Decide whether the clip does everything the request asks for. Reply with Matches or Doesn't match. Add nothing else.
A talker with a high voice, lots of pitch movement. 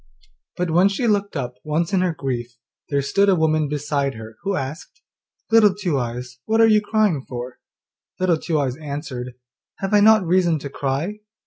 Doesn't match